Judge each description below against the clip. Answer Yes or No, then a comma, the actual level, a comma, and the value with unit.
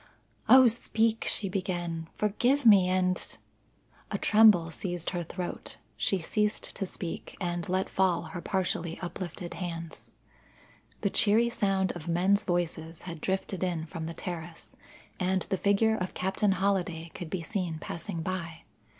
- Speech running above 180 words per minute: No, average, 150 wpm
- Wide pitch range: No, average, 2.7 semitones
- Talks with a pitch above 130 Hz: Yes, medium, 185 Hz